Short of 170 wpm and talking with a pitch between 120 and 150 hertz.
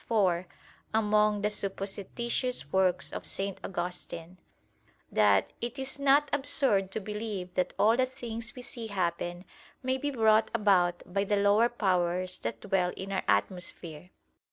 No: average, 145 wpm; high, 200 Hz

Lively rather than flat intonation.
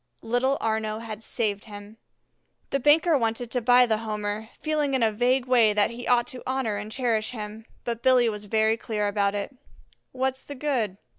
No: average, 3.0 semitones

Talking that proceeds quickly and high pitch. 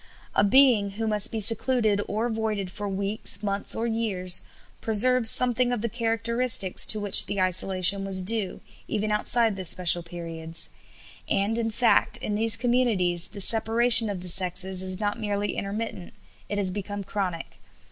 No: average, 160 wpm; high, 205 Hz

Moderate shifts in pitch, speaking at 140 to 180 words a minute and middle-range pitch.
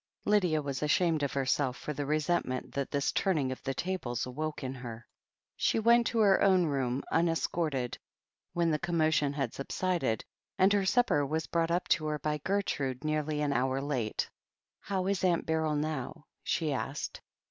Yes: average, 4.1 semitones; average, 170 wpm; medium, 150 Hz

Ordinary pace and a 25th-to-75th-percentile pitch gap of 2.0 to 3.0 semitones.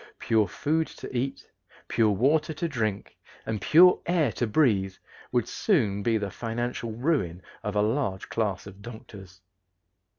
No: average, 145 wpm; wide, 5.6 semitones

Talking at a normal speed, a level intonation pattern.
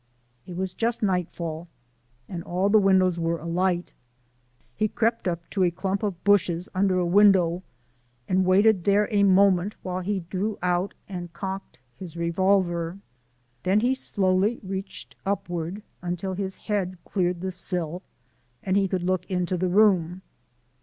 Yes: average, 150 wpm; narrow, 2.1 semitones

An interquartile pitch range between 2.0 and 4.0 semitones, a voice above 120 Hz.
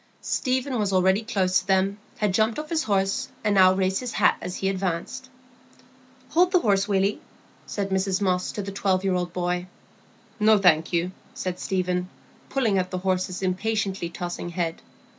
Yes: narrow, 2.4 semitones; high, 190 Hz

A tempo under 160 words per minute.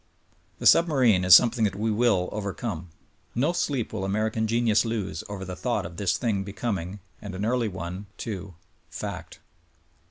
No: average, 165 wpm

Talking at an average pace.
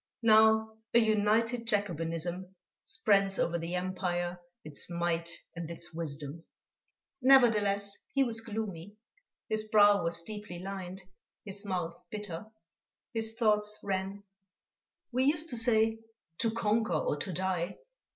No: slow, 120 wpm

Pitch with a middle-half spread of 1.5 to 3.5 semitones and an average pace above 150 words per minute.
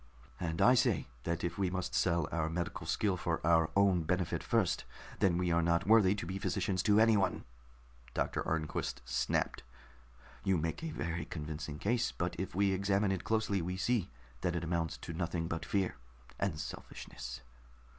Yes: average, 2.8 semitones; average, 175 wpm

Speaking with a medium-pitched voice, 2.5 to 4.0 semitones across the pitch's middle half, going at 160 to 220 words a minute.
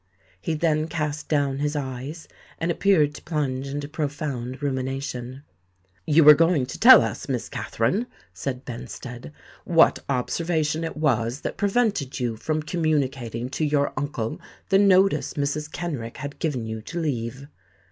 No: medium, 145 Hz; average, 3.7 semitones; average, 145 wpm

